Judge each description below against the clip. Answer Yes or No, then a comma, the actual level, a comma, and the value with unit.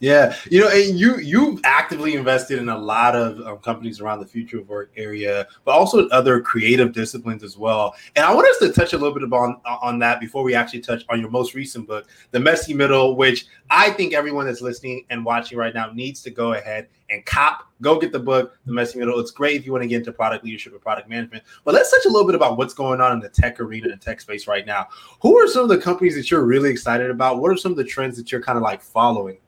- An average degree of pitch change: Yes, average, 3.1 semitones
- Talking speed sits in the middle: No, fast, 265 wpm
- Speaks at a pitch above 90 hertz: Yes, low, 125 Hz